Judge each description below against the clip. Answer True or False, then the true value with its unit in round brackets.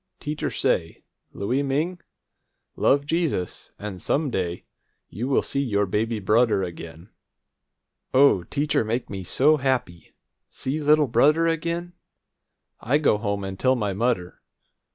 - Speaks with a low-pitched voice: True (125 Hz)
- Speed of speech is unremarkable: False (130 wpm)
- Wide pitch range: True (6.6 semitones)